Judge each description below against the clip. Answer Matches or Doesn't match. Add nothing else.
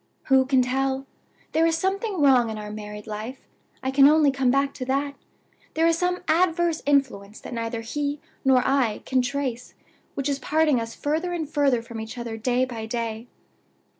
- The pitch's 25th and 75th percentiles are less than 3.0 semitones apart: Doesn't match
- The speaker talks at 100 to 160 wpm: Doesn't match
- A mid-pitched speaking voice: Doesn't match